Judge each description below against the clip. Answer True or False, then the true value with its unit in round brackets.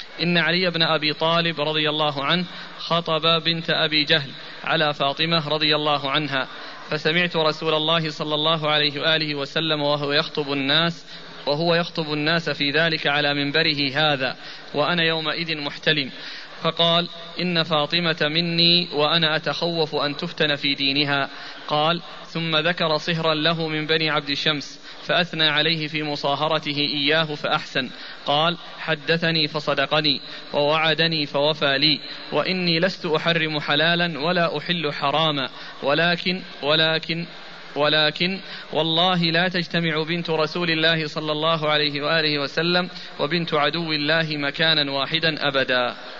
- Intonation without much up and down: True (1.9 semitones)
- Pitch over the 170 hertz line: False (155 Hz)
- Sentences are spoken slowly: False (125 wpm)